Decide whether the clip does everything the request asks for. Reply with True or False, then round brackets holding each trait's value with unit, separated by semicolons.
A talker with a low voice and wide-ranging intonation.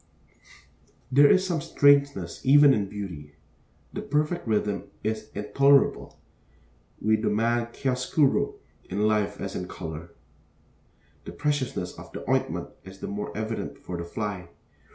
True (110 Hz; 6.1 semitones)